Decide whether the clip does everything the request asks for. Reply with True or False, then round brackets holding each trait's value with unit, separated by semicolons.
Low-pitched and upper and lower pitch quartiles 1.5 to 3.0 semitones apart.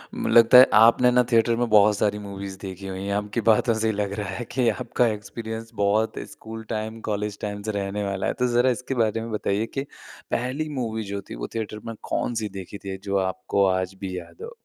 True (110 Hz; 2.6 semitones)